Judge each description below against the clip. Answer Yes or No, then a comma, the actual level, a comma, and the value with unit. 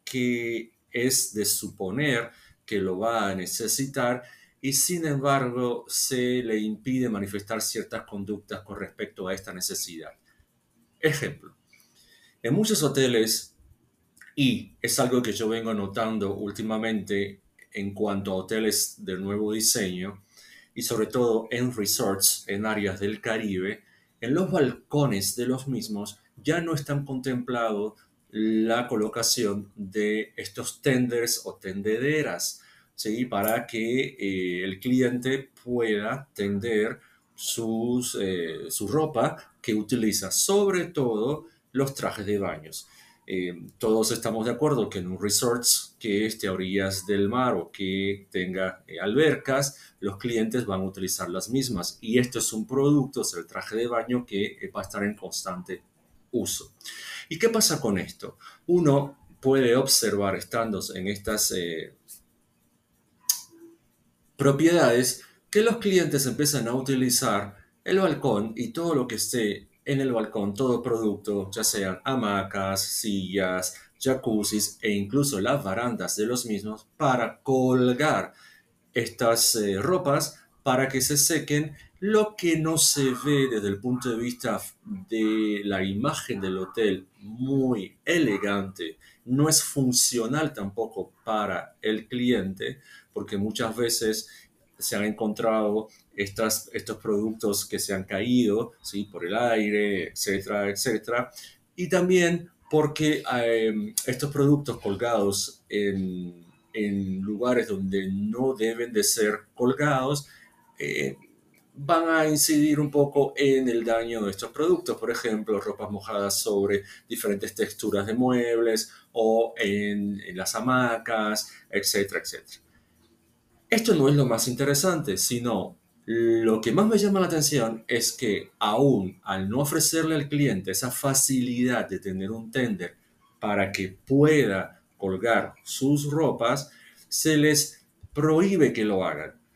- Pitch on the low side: Yes, low, 115 Hz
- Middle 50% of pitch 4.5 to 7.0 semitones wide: Yes, average, 5.0 semitones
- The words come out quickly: No, average, 135 wpm